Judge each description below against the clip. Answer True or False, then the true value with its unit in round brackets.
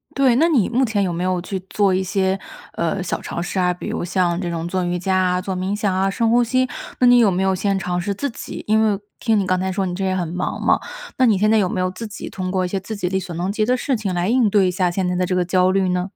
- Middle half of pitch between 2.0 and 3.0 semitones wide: True (2.7 semitones)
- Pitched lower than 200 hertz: True (190 Hz)